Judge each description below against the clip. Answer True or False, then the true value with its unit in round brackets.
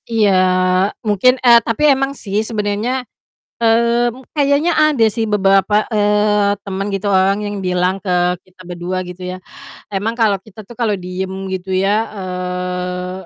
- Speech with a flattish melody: False (3.3 semitones)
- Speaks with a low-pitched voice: False (200 Hz)